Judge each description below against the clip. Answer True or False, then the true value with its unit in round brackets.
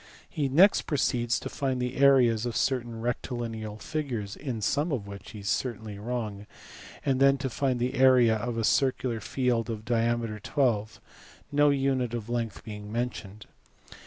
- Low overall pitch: True (120 Hz)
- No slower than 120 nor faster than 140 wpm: False (160 wpm)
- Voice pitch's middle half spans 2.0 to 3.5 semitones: True (3.2 semitones)